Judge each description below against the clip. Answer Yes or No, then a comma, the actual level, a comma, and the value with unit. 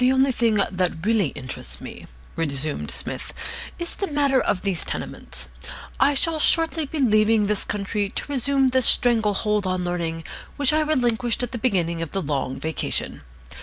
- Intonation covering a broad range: Yes, wide, 6.7 semitones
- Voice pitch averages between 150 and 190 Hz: No, high, 215 Hz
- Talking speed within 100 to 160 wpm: No, average, 170 wpm